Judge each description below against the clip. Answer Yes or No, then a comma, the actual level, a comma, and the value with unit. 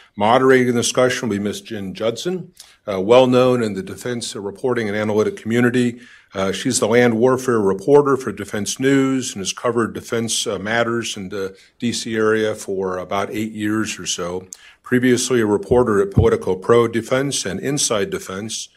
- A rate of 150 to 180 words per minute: Yes, average, 170 wpm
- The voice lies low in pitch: Yes, low, 115 Hz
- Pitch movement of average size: Yes, average, 3.5 semitones